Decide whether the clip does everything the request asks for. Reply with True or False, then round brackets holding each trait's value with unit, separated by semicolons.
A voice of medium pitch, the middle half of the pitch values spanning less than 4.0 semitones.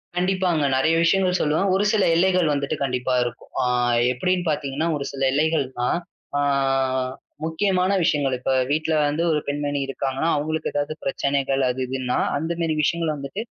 True (150 Hz; 3.5 semitones)